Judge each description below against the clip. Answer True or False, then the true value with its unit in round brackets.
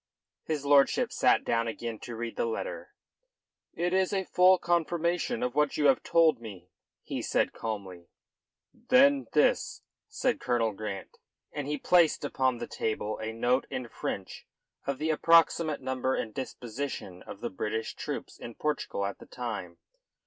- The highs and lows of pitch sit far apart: True (6.8 semitones)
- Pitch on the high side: False (130 Hz)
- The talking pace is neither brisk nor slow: True (155 wpm)